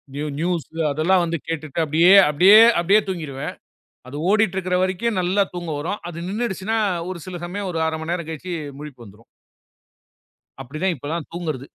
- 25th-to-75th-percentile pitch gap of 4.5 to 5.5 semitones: No, average, 3.5 semitones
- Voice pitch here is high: No, medium, 170 Hz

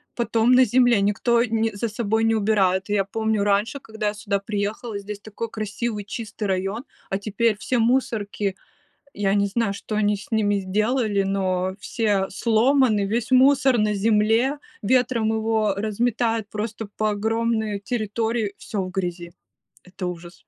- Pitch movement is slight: Yes, narrow, 2.3 semitones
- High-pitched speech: Yes, high, 215 Hz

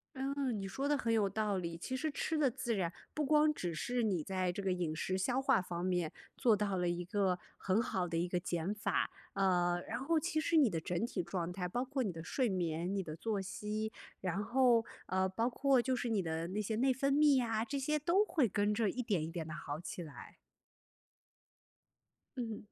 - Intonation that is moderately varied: No, wide, 6.3 semitones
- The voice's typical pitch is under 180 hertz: No, high, 205 Hz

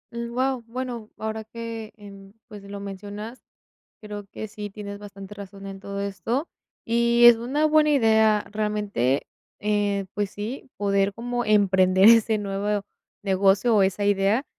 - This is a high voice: Yes, high, 210 Hz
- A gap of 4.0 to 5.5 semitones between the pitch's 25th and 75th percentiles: No, narrow, 2.6 semitones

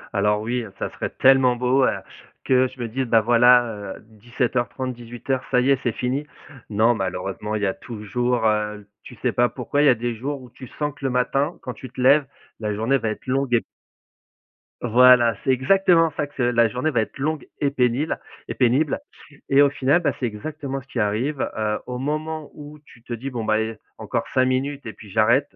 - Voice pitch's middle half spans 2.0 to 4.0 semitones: Yes, average, 3.3 semitones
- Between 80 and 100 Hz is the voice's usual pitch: No, low, 125 Hz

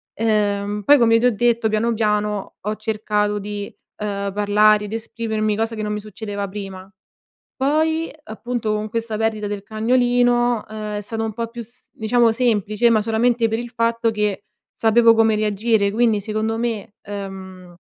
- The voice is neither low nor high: No, high, 215 Hz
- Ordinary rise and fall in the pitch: No, narrow, 1.8 semitones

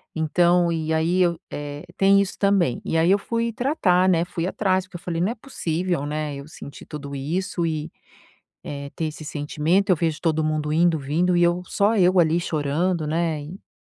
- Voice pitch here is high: No, medium, 170 Hz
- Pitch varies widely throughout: No, average, 3.1 semitones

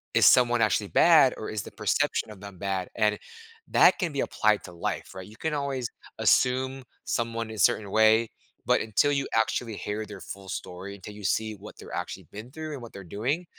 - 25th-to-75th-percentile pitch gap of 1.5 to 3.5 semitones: No, average, 3.9 semitones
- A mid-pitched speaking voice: No, low, 110 Hz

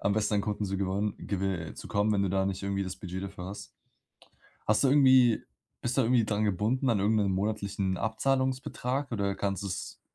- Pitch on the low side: Yes, low, 100 Hz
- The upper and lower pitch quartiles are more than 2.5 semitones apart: Yes, average, 2.9 semitones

